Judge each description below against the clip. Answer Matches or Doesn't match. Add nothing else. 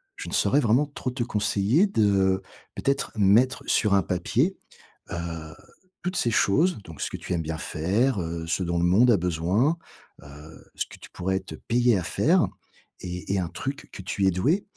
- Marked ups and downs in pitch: Matches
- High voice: Doesn't match